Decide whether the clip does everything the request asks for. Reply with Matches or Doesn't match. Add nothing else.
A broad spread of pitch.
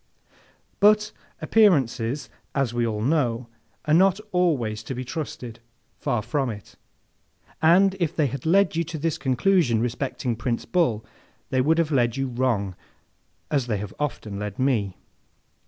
Matches